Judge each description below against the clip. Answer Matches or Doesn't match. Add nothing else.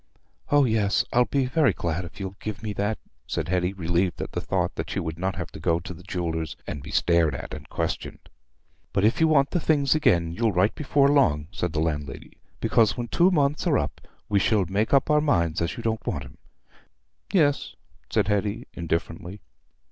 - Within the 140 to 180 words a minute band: Doesn't match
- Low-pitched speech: Matches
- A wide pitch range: Matches